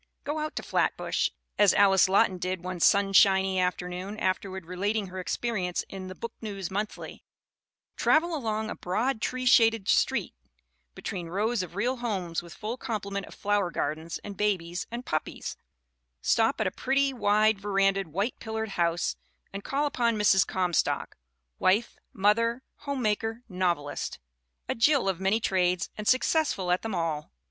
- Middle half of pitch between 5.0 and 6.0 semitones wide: No, average, 3.7 semitones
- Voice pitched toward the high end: Yes, high, 200 Hz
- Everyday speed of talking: Yes, average, 160 wpm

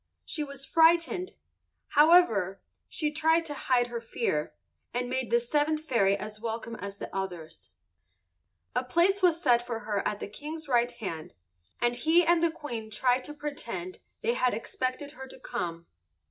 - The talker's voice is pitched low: No, very high, 250 Hz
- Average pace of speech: Yes, average, 165 wpm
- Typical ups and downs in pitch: No, wide, 5.8 semitones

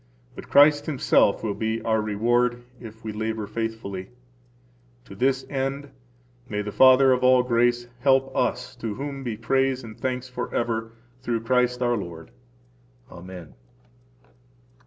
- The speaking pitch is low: Yes, low, 120 Hz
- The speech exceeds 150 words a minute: No, slow, 135 wpm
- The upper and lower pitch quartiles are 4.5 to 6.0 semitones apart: No, average, 2.8 semitones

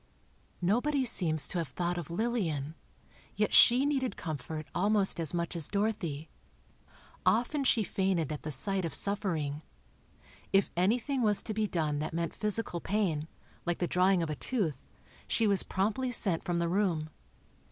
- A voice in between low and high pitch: Yes, medium, 180 Hz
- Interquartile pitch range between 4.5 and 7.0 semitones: Yes, average, 4.9 semitones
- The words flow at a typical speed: Yes, average, 160 wpm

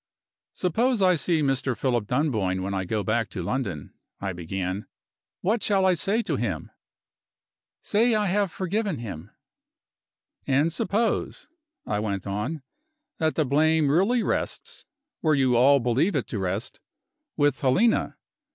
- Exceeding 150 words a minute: No, average, 140 wpm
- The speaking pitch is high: No, medium, 140 Hz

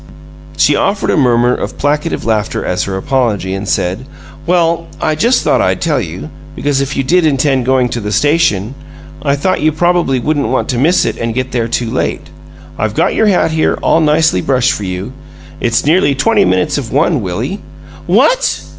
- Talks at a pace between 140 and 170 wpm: No, average, 190 wpm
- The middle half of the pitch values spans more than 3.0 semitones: Yes, wide, 5.5 semitones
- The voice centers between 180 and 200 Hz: No, low, 135 Hz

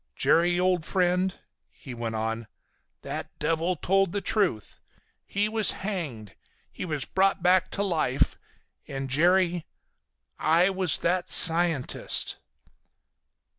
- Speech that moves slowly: Yes, slow, 110 wpm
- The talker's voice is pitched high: No, medium, 175 Hz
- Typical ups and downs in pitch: Yes, average, 3.9 semitones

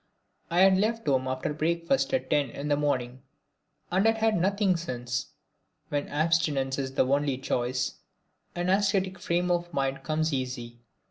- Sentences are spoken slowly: No, average, 155 wpm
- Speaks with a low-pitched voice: No, medium, 150 Hz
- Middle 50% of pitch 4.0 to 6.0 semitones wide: Yes, average, 5.3 semitones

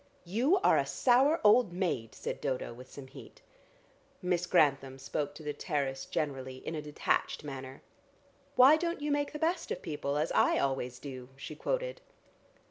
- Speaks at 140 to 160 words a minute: No, average, 170 wpm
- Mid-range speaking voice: Yes, medium, 150 Hz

